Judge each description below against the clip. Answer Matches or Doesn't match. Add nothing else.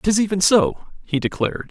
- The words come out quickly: Doesn't match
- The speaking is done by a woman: Doesn't match